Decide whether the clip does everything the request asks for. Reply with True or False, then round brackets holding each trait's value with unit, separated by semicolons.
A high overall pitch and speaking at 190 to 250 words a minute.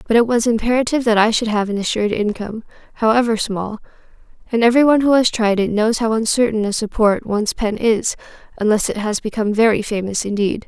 True (220 Hz; 195 wpm)